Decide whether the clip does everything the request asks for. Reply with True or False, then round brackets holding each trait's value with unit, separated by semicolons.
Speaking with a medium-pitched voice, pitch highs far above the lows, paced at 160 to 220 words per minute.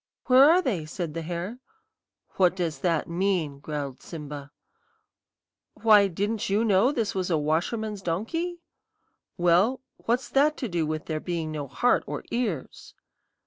False (180 Hz; 6.2 semitones; 145 wpm)